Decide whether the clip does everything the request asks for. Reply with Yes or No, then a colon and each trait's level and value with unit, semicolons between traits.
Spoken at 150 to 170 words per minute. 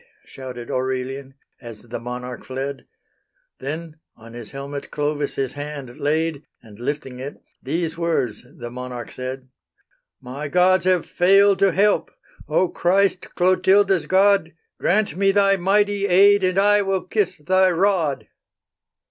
No: slow, 135 wpm